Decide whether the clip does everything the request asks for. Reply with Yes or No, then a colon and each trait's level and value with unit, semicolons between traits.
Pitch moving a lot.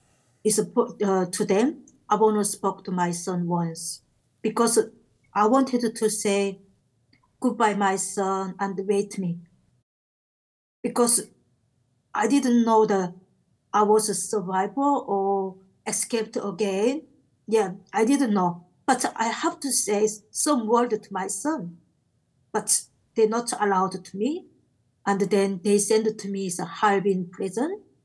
No: average, 3.1 semitones